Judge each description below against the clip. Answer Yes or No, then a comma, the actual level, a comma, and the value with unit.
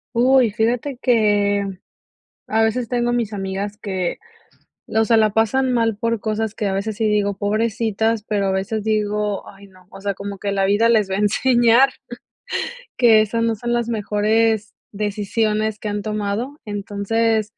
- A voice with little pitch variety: Yes, narrow, 2.0 semitones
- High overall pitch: Yes, high, 215 Hz